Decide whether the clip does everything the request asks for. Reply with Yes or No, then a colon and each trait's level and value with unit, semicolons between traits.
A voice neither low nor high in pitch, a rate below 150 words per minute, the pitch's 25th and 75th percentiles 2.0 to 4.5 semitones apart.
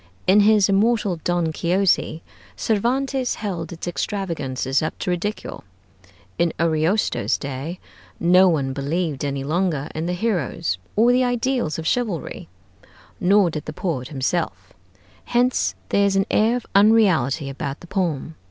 No: medium, 175 Hz; average, 140 wpm; average, 5.2 semitones